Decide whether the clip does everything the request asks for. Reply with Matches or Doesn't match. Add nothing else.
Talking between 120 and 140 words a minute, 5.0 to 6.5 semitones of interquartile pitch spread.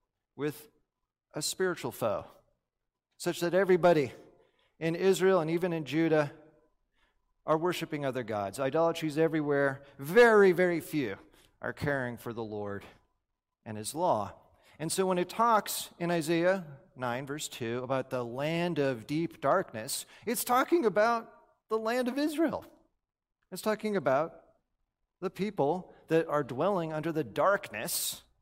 Matches